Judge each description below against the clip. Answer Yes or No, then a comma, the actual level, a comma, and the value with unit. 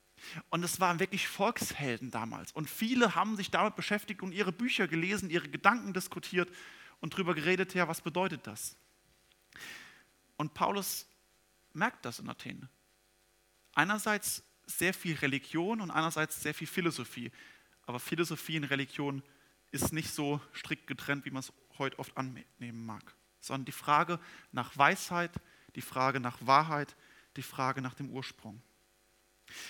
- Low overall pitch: No, medium, 155 Hz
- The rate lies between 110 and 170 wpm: Yes, average, 145 wpm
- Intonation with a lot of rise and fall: Yes, wide, 5.8 semitones